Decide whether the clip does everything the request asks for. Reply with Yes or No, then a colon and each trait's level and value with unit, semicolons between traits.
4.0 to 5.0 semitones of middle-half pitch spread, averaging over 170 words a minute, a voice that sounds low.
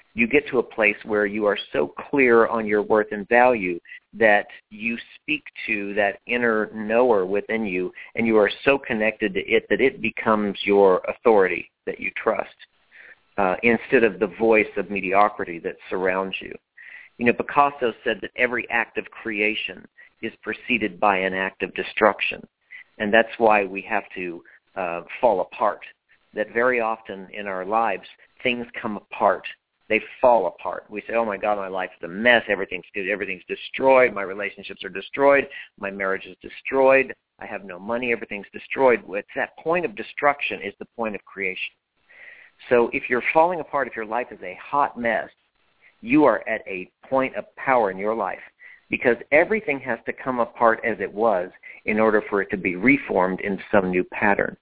No: average, 3.4 semitones; average, 180 wpm; low, 110 Hz